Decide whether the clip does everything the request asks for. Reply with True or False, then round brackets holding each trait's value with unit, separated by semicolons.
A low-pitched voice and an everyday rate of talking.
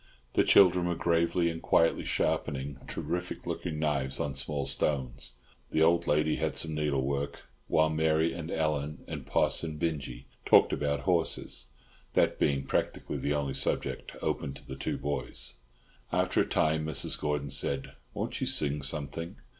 True (75 Hz; 155 wpm)